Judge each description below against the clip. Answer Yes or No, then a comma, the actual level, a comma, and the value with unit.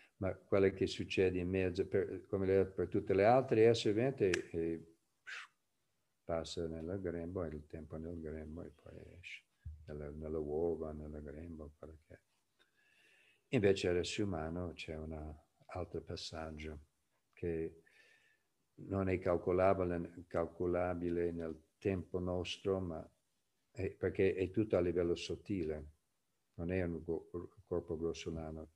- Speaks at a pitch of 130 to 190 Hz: No, very low, 85 Hz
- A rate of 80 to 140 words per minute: Yes, average, 125 wpm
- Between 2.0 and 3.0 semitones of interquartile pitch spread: Yes, narrow, 2.5 semitones